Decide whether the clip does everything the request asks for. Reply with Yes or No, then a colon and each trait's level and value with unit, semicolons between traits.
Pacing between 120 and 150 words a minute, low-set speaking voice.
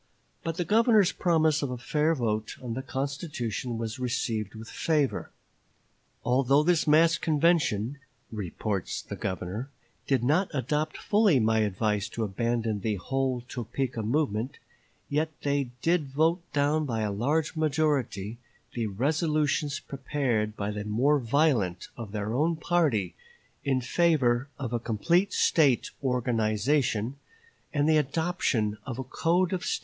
Yes: average, 140 wpm; low, 130 Hz